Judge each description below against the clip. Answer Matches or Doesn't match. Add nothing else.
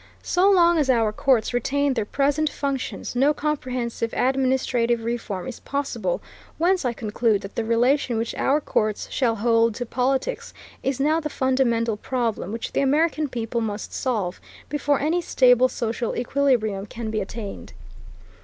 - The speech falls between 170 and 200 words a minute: Doesn't match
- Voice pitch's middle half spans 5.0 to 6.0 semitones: Doesn't match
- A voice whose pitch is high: Matches